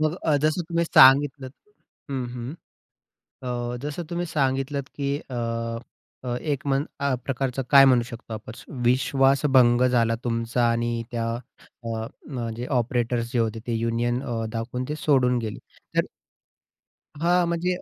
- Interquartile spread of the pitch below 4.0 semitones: Yes, average, 3.0 semitones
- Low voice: Yes, low, 125 Hz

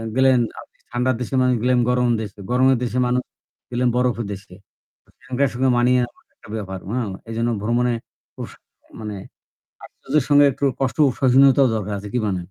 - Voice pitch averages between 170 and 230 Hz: No, low, 125 Hz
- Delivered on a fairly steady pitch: Yes, narrow, 2.3 semitones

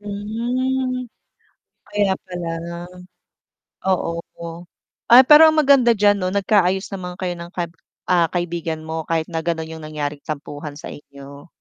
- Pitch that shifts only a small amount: No, average, 5.0 semitones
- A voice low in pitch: No, medium, 180 Hz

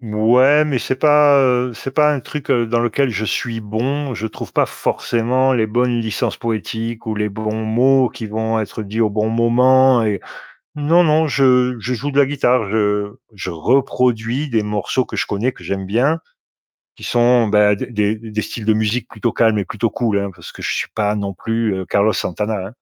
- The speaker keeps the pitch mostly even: No, average, 3.1 semitones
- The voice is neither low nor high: No, low, 115 Hz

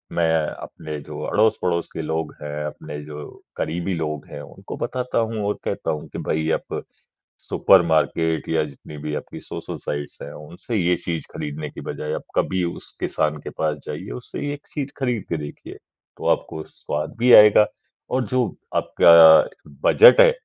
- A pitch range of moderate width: No, wide, 5.8 semitones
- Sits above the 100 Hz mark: No, very low, 80 Hz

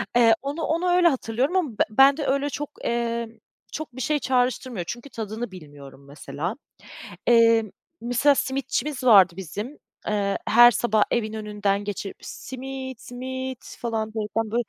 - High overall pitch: Yes, high, 240 Hz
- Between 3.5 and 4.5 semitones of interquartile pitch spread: Yes, average, 3.9 semitones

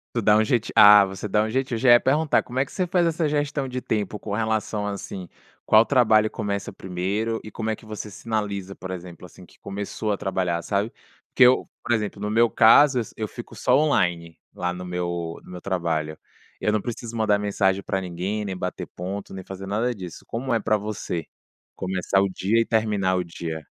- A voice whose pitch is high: No, low, 105 Hz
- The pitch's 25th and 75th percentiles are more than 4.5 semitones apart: No, average, 3.5 semitones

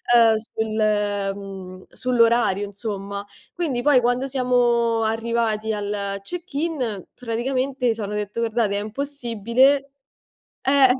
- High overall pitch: Yes, high, 230 Hz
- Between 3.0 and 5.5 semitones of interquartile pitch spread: Yes, average, 3.5 semitones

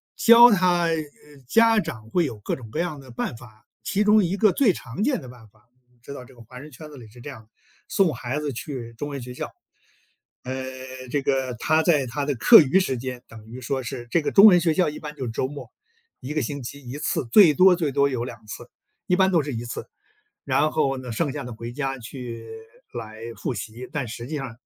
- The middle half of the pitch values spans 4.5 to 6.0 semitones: Yes, average, 4.9 semitones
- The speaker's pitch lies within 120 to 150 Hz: Yes, low, 135 Hz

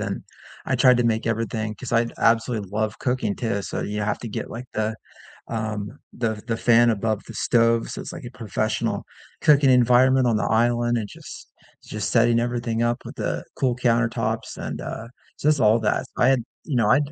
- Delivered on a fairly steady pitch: Yes, narrow, 1.8 semitones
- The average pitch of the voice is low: Yes, low, 115 Hz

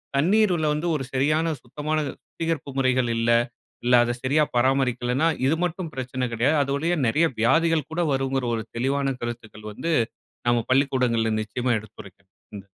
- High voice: No, low, 135 Hz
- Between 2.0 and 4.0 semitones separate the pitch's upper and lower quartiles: No, average, 4.5 semitones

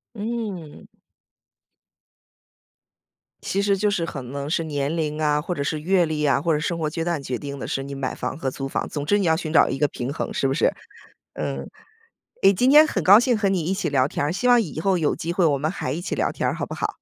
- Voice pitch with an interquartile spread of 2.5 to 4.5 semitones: No, average, 5.1 semitones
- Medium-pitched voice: Yes, medium, 160 Hz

